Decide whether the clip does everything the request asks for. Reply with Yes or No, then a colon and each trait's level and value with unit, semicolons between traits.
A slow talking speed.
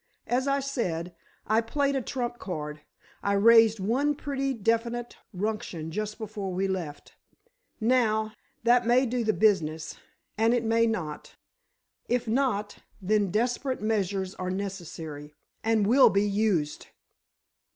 Yes: slow, 120 wpm